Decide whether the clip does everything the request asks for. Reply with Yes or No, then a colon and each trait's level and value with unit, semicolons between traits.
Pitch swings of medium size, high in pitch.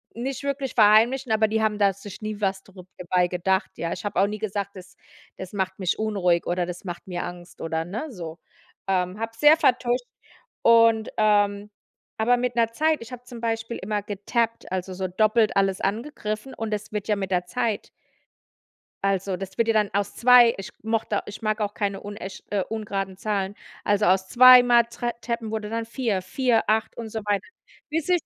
Yes: average, 3.2 semitones; high, 210 Hz